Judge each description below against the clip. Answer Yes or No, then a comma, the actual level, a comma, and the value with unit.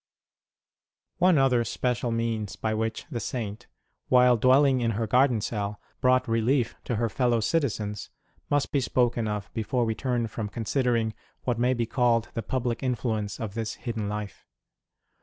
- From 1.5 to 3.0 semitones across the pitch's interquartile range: Yes, narrow, 2.5 semitones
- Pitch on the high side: No, low, 115 Hz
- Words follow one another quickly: No, average, 160 wpm